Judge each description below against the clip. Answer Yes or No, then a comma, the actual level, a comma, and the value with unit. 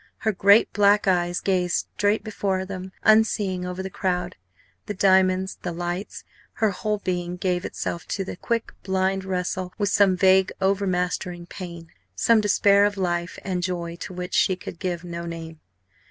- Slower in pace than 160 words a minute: No, average, 165 wpm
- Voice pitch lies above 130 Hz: Yes, medium, 185 Hz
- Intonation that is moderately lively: No, narrow, 2.0 semitones